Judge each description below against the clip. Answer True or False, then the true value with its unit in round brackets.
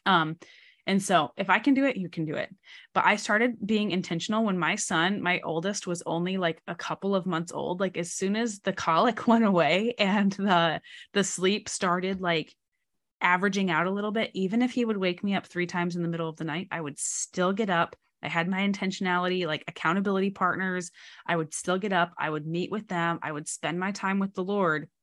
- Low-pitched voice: False (185 Hz)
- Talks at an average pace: False (225 wpm)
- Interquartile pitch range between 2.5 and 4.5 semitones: True (2.9 semitones)